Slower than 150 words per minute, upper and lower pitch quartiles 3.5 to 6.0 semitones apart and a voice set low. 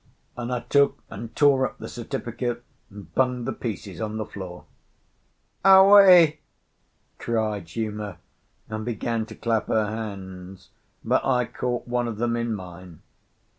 No: average, 140 wpm; average, 3.0 semitones; low, 115 Hz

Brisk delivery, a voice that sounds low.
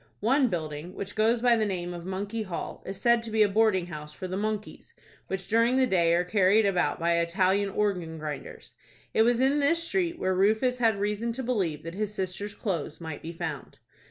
No: fast, 210 wpm; high, 200 Hz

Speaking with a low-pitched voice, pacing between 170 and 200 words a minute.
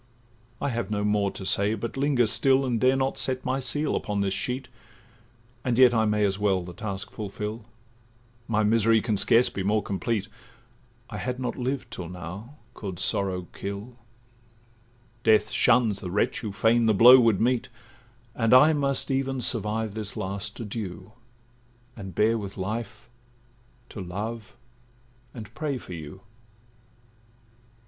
No: low, 110 Hz; average, 155 wpm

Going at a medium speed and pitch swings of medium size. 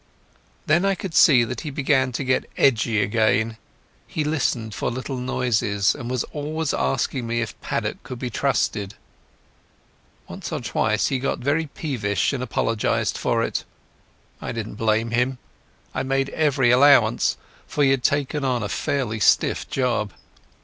Yes: average, 155 wpm; average, 3.6 semitones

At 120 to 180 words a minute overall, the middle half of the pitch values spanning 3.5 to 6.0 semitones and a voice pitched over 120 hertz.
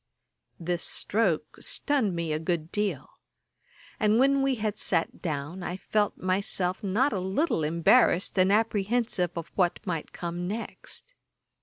Yes: average, 140 wpm; average, 4.2 semitones; high, 190 Hz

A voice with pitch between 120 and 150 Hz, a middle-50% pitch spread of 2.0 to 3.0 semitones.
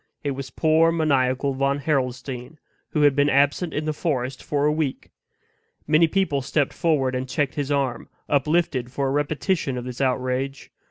Yes: medium, 140 Hz; average, 2.7 semitones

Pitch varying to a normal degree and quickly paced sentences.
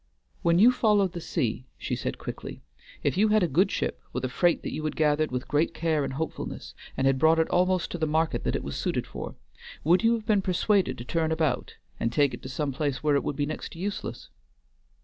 Yes: average, 4.3 semitones; fast, 240 wpm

